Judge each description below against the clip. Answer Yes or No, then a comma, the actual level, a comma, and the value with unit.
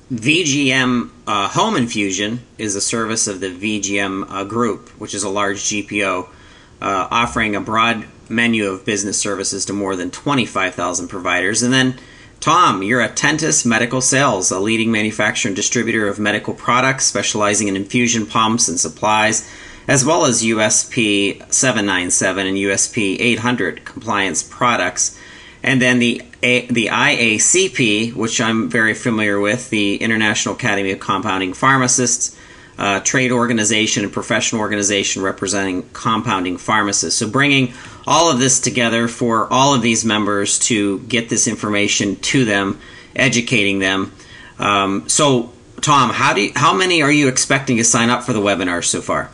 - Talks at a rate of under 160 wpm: Yes, average, 150 wpm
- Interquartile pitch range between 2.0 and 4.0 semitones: Yes, average, 3.3 semitones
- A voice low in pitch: Yes, low, 110 Hz